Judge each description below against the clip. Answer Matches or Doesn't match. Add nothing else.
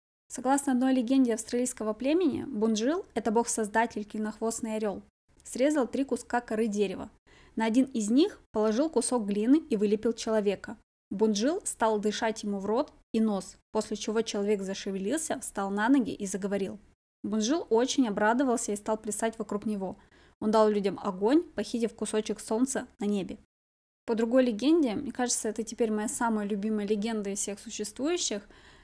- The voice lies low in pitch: Doesn't match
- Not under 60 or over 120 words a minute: Doesn't match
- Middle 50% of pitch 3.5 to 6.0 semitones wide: Doesn't match